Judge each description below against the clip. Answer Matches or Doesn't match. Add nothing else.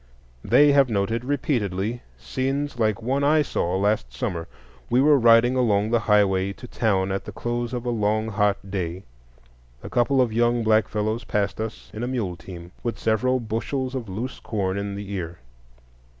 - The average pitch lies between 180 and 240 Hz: Doesn't match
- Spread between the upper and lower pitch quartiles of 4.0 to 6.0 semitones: Doesn't match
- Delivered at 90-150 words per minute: Doesn't match